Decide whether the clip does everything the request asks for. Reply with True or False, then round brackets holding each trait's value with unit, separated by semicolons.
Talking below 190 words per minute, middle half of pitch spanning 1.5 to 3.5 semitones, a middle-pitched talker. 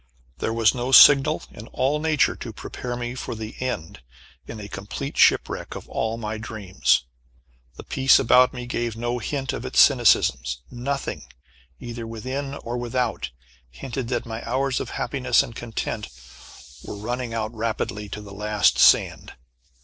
False (155 wpm; 2.9 semitones; 120 Hz)